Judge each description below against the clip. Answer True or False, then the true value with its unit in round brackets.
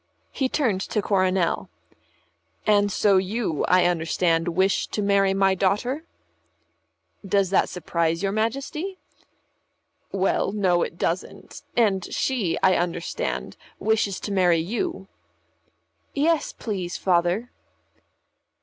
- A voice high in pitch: True (195 Hz)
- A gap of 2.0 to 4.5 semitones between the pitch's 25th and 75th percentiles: True (3.6 semitones)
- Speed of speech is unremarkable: False (110 wpm)